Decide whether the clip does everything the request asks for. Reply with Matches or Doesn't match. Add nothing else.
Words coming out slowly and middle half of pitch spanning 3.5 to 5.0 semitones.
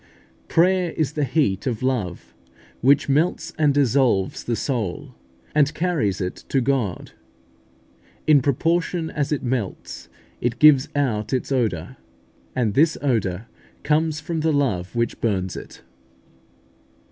Doesn't match